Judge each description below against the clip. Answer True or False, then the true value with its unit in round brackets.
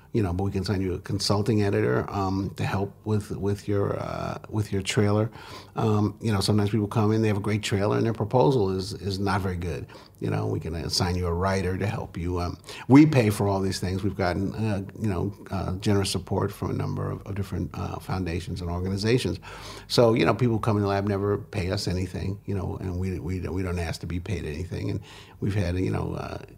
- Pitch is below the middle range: True (100 Hz)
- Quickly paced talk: True (240 wpm)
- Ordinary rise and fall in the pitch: False (1.9 semitones)